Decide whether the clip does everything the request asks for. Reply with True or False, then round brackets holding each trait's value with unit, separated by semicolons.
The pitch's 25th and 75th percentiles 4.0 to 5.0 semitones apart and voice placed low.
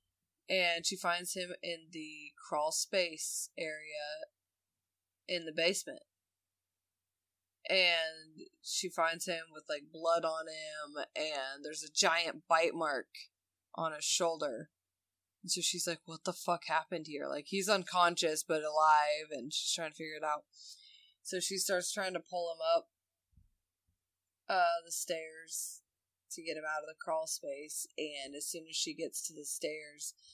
False (4.4 semitones; 160 Hz)